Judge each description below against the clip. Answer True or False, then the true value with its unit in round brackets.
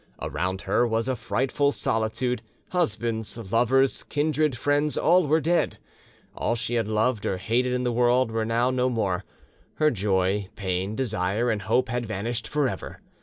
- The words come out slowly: False (165 wpm)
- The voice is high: False (120 Hz)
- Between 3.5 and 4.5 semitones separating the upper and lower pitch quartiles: False (3.1 semitones)